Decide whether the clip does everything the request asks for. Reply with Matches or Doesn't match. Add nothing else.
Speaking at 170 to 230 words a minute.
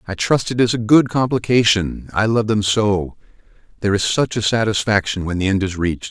Matches